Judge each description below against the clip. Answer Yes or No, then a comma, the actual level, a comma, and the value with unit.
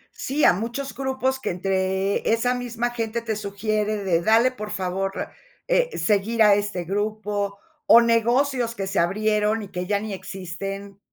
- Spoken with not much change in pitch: No, average, 3.2 semitones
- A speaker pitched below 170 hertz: No, high, 210 Hz